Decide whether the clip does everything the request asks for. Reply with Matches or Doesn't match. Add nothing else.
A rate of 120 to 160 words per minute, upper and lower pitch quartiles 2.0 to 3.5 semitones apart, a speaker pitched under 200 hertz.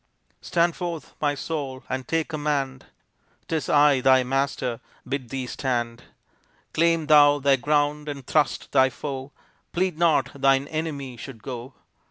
Matches